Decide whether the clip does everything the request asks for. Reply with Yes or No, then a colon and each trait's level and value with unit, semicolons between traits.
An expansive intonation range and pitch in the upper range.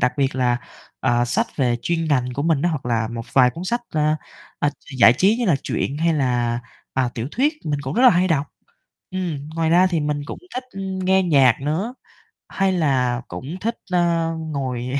No: wide, 5.9 semitones; medium, 150 Hz